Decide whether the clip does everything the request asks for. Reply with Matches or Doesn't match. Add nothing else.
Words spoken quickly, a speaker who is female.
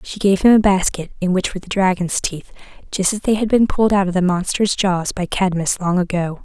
Matches